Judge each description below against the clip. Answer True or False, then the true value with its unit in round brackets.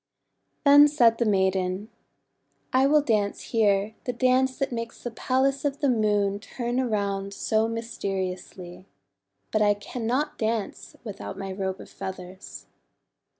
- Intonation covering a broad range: False (4.4 semitones)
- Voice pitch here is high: True (220 Hz)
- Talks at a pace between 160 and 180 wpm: False (135 wpm)